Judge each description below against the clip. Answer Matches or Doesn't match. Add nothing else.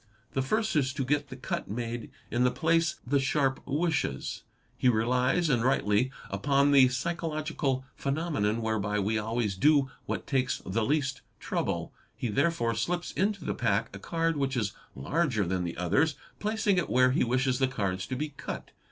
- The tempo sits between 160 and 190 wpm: Matches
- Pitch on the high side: Doesn't match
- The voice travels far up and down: Doesn't match